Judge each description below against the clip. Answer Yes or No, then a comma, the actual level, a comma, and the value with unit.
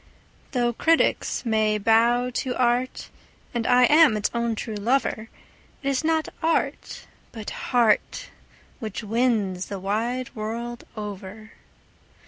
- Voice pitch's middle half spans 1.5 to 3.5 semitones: Yes, average, 2.8 semitones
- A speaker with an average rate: No, slow, 120 wpm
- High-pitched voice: Yes, high, 235 Hz